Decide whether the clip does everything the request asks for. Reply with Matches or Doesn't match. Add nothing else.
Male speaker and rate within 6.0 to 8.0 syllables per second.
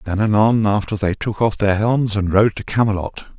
Doesn't match